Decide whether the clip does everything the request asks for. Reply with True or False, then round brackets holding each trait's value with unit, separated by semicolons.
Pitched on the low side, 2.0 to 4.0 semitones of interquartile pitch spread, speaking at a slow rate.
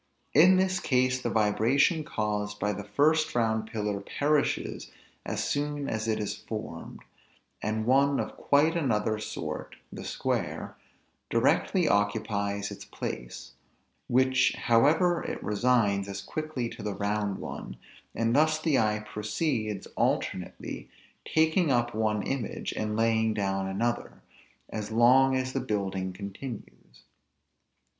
False (110 Hz; 4.9 semitones; 130 wpm)